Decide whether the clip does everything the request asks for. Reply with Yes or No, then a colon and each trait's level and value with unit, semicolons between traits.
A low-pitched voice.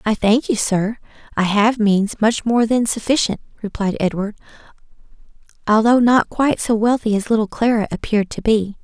No: high, 220 Hz